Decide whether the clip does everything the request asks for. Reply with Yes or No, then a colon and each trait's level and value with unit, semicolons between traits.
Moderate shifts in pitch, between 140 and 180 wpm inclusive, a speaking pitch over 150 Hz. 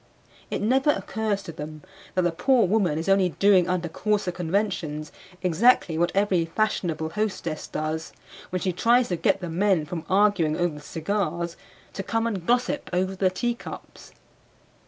Yes: average, 4.1 semitones; average, 160 wpm; medium, 185 Hz